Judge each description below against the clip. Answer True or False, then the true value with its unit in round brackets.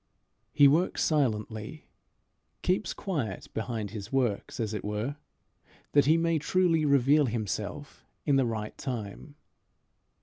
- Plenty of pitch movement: True (5.7 semitones)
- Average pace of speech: False (125 wpm)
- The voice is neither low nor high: False (130 Hz)